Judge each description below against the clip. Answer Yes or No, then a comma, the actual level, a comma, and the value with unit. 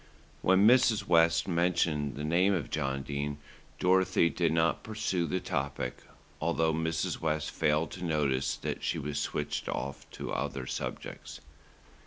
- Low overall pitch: Yes, very low, 80 Hz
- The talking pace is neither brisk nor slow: Yes, average, 145 wpm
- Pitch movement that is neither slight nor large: Yes, average, 3.5 semitones